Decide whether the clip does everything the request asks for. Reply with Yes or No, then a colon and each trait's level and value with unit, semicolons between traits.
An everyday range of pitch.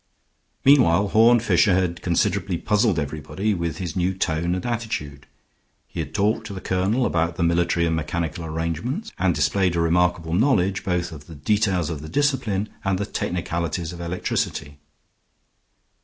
Yes: average, 3.5 semitones